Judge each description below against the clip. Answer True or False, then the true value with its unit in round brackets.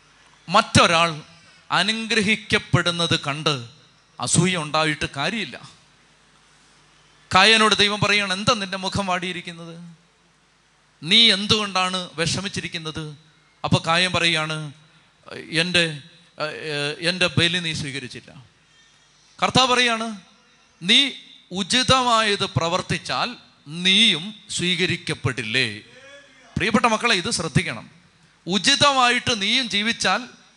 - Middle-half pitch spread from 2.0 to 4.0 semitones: False (5.1 semitones)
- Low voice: False (175 Hz)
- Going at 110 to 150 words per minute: False (75 wpm)